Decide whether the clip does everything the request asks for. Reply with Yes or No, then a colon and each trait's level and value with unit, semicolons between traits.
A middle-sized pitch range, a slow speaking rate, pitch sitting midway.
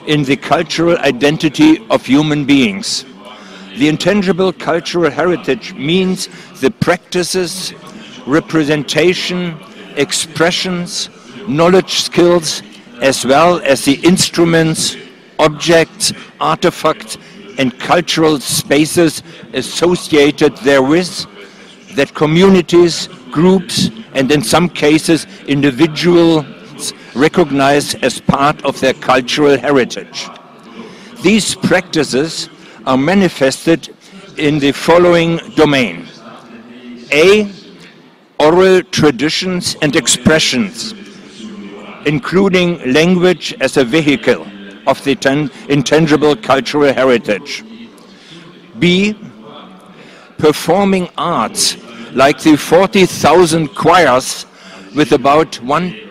Yes: average, 4.2 semitones; slow, 85 wpm; medium, 165 Hz